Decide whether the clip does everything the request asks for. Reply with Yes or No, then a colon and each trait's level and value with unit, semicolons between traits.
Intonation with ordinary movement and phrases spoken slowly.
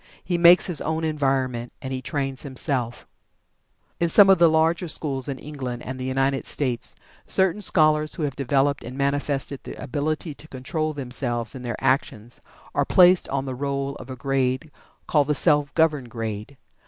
No: average, 3.1 semitones; average, 175 wpm